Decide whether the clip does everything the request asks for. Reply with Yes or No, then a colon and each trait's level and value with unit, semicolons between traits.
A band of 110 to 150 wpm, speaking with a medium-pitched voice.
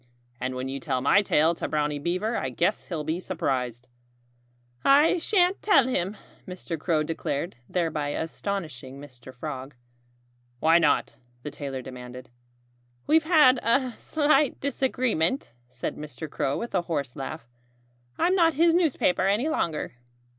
Yes: average, 140 wpm; medium, 165 Hz